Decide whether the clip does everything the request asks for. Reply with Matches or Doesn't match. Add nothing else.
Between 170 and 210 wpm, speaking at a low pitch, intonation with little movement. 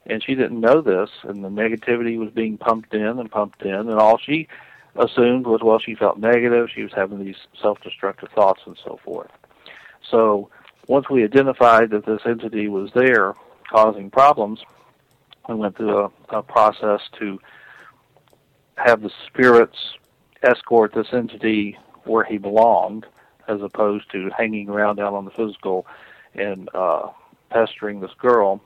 Doesn't match